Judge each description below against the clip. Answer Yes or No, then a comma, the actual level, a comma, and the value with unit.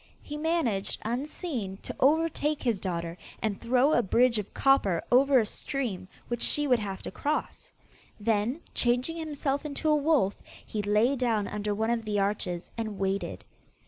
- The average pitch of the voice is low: No, high, 235 Hz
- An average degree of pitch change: No, wide, 5.7 semitones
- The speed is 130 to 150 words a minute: No, average, 165 wpm